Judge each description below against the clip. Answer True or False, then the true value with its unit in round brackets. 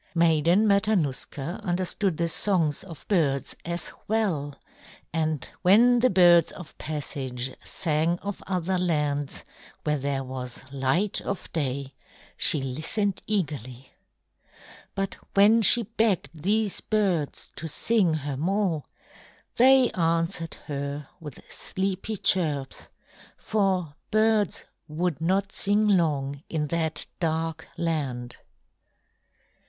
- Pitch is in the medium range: True (165 Hz)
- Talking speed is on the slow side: True (110 wpm)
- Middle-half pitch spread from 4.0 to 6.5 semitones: True (5.2 semitones)